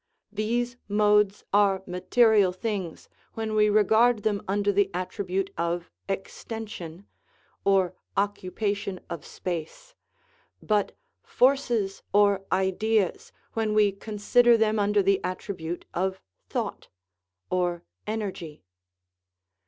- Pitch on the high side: Yes, high, 200 Hz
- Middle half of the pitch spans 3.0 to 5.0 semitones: No, narrow, 2.5 semitones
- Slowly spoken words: Yes, slow, 110 wpm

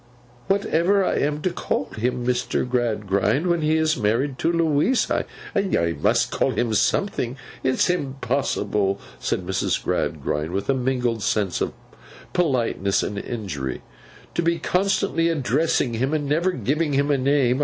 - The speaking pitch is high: No, low, 135 Hz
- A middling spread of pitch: No, wide, 6.2 semitones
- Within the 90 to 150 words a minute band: Yes, average, 145 wpm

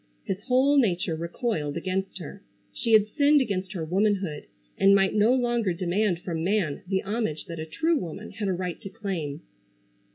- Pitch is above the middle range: Yes, high, 195 Hz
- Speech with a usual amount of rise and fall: Yes, average, 4.2 semitones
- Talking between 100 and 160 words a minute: No, average, 175 wpm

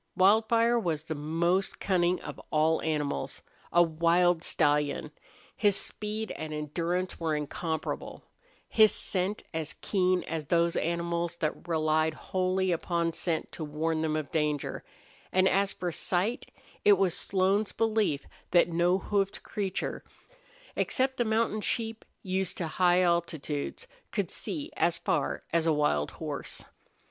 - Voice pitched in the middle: Yes, medium, 175 Hz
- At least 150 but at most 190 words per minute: No, slow, 135 wpm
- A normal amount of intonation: Yes, average, 3.5 semitones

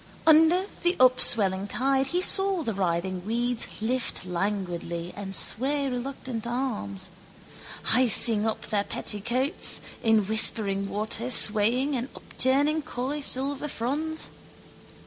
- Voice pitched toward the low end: No, high, 240 Hz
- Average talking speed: No, slow, 110 wpm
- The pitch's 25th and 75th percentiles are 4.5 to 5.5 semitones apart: Yes, average, 5.1 semitones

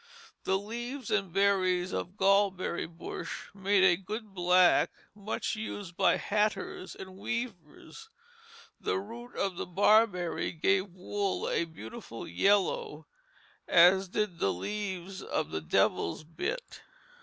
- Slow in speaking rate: Yes, slow, 125 wpm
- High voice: Yes, high, 195 Hz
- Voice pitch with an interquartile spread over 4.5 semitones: No, average, 2.9 semitones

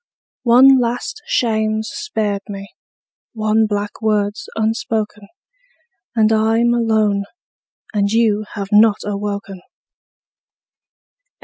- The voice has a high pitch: Yes, high, 215 Hz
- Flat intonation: Yes, narrow, 1.7 semitones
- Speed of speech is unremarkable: No, slow, 90 wpm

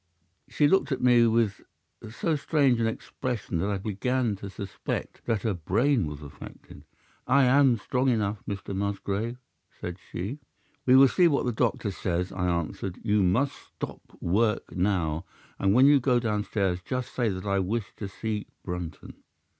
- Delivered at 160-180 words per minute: Yes, average, 165 wpm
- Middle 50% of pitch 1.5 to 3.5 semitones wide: No, average, 4.5 semitones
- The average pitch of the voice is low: Yes, low, 105 Hz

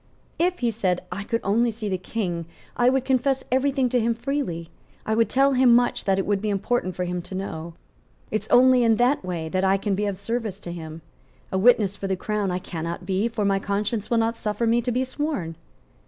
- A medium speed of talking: No, fast, 235 wpm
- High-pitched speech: Yes, high, 210 Hz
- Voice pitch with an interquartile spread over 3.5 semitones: Yes, average, 4.4 semitones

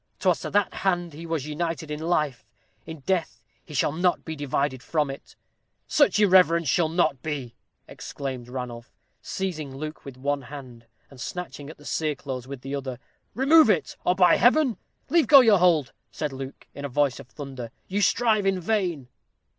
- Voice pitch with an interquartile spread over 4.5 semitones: Yes, average, 4.9 semitones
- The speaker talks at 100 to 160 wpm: No, average, 180 wpm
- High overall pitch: No, medium, 155 Hz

